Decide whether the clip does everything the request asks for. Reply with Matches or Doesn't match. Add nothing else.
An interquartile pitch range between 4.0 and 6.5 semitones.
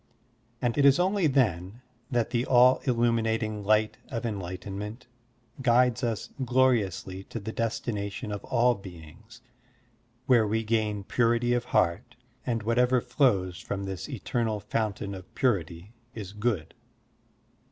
Doesn't match